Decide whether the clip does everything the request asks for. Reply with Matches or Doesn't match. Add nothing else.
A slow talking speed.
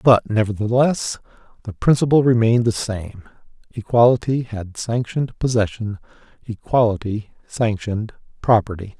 Matches